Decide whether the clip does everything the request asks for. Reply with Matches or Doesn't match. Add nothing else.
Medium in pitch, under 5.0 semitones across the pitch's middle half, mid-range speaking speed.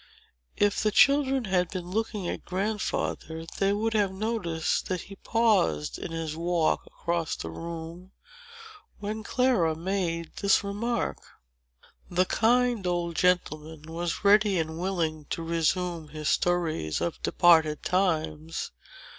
Doesn't match